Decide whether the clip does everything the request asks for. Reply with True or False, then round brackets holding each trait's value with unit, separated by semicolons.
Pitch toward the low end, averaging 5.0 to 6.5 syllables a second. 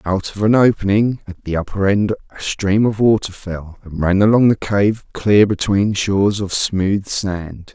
False (100 Hz; 4.3 syllables/s)